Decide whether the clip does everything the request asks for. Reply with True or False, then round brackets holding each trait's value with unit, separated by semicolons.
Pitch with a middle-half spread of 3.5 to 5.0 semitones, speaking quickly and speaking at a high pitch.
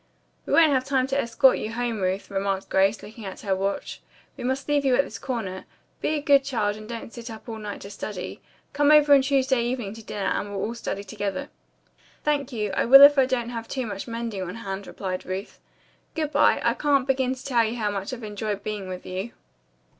True (4.7 semitones; 225 wpm; 230 Hz)